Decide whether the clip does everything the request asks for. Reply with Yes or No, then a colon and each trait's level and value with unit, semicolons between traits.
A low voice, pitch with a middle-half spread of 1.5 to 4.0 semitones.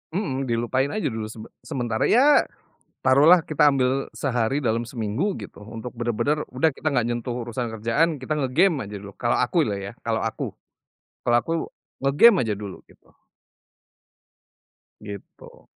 No: low, 125 Hz; average, 4.8 semitones